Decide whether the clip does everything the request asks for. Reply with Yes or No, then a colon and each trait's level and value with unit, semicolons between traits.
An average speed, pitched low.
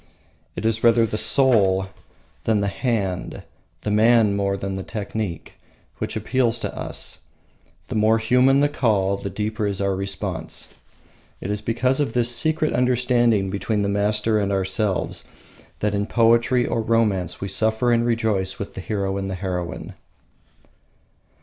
Yes: average, 150 wpm; low, 105 Hz